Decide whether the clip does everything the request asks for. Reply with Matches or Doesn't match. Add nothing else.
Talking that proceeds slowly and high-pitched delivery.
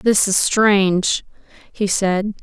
Matches